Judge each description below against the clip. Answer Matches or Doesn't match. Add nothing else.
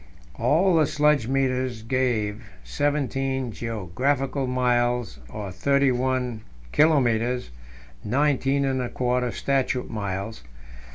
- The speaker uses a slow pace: Matches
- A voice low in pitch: Matches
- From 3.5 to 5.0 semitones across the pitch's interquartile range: Doesn't match